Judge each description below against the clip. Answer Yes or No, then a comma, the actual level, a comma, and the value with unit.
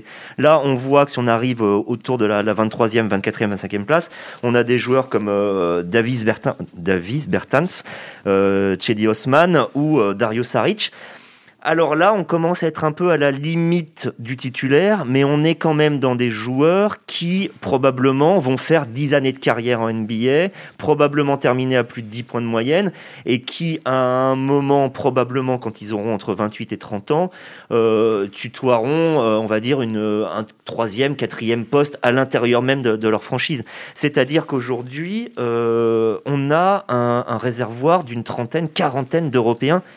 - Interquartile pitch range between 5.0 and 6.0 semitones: No, average, 4.4 semitones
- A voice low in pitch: Yes, low, 125 Hz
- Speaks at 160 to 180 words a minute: Yes, average, 170 wpm